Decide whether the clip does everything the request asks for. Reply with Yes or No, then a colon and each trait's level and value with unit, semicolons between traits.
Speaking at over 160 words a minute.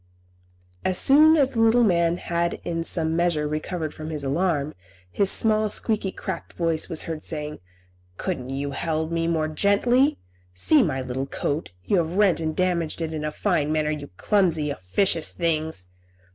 Yes: average, 175 wpm